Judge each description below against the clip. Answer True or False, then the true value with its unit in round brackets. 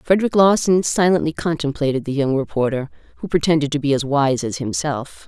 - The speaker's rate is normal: True (170 wpm)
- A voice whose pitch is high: False (150 Hz)